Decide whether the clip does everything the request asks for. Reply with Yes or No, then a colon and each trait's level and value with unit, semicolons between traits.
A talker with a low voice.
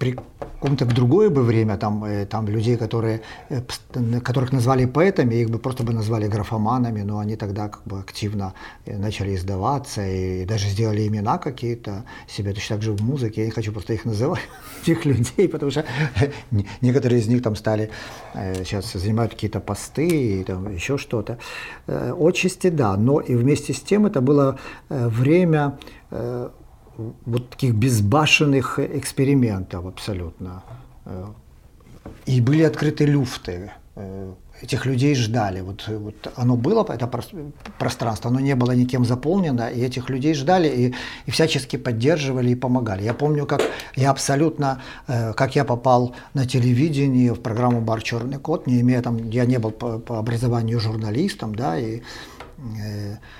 Yes: low, 120 Hz